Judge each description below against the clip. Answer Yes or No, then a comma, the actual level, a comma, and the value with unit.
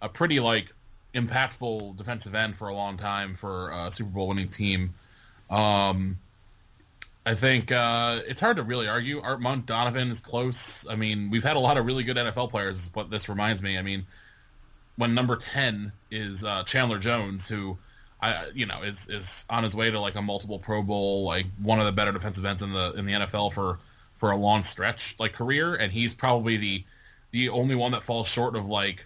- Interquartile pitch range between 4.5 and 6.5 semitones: No, average, 3.1 semitones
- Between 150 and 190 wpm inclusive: No, fast, 205 wpm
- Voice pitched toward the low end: Yes, low, 105 Hz